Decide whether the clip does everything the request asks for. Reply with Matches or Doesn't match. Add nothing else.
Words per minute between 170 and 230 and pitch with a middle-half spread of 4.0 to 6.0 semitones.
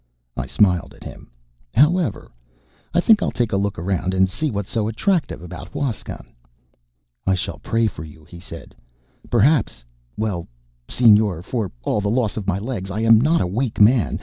Matches